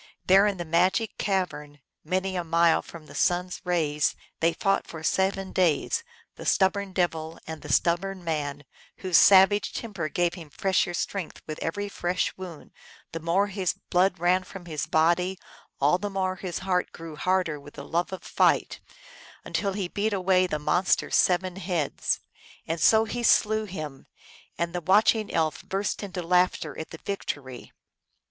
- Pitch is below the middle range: No, medium, 180 Hz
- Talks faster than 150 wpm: Yes, average, 170 wpm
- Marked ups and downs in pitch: No, average, 2.9 semitones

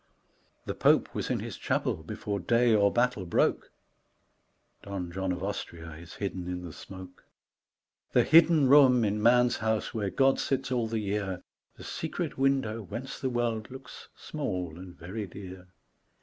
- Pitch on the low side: Yes, low, 105 Hz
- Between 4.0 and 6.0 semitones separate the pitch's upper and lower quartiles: Yes, average, 5.1 semitones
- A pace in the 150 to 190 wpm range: Yes, average, 160 wpm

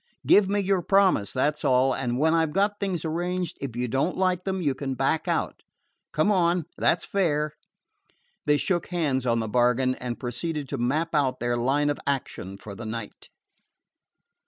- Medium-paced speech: Yes, average, 190 wpm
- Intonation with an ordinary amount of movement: No, wide, 5.8 semitones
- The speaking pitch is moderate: Yes, medium, 145 Hz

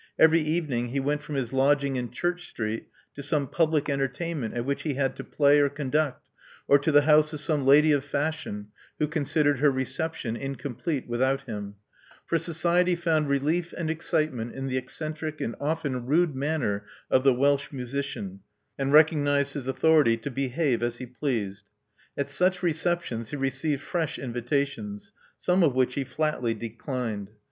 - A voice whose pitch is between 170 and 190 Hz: No, medium, 140 Hz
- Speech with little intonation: No, average, 3.4 semitones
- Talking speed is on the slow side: No, average, 170 wpm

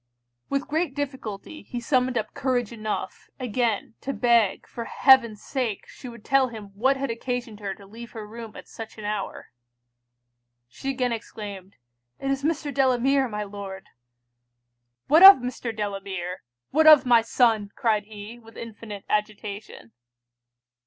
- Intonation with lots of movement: No, average, 3.9 semitones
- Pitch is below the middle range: No, high, 230 Hz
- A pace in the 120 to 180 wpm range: Yes, average, 150 wpm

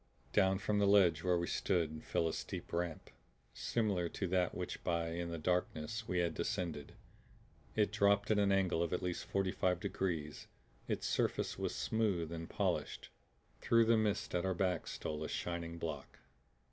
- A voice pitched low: Yes, very low, 90 Hz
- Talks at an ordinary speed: Yes, average, 175 wpm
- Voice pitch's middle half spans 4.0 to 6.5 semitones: No, average, 3.0 semitones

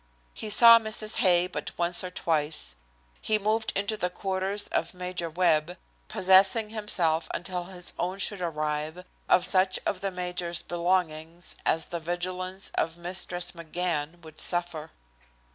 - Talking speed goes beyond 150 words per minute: No, average, 145 wpm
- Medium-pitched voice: Yes, medium, 180 Hz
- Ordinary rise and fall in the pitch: No, narrow, 2.0 semitones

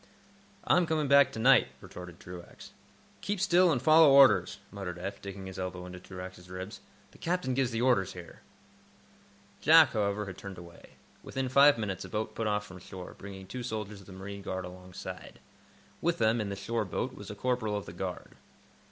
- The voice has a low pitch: Yes, low, 105 Hz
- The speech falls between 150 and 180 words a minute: No, average, 190 wpm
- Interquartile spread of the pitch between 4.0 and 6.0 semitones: Yes, wide, 5.5 semitones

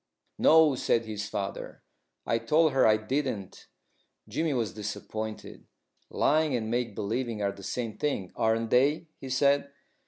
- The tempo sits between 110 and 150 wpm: Yes, average, 145 wpm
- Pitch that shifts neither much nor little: Yes, average, 4.6 semitones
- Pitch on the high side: No, low, 115 Hz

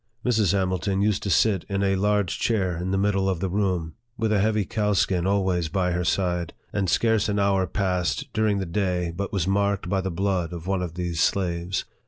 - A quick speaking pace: Yes, fast, 210 wpm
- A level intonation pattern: Yes, narrow, 2.2 semitones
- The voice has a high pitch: No, very low, 95 Hz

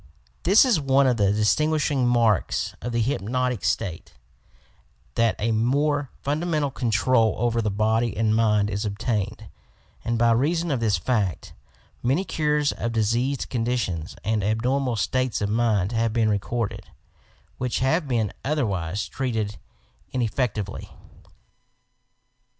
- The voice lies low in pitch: Yes, low, 115 Hz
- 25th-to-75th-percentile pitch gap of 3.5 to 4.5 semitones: Yes, average, 3.8 semitones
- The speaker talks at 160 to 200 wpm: No, average, 140 wpm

